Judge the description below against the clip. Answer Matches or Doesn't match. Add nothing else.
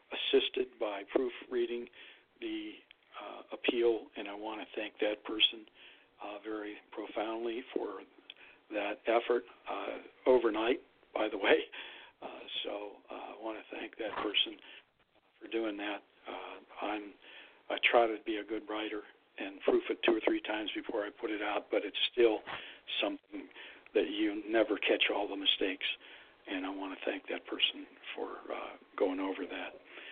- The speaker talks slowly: Doesn't match